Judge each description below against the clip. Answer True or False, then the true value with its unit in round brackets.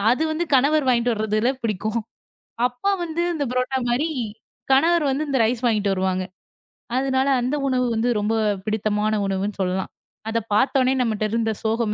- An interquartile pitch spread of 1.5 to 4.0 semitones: True (3.7 semitones)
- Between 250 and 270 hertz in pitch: False (235 Hz)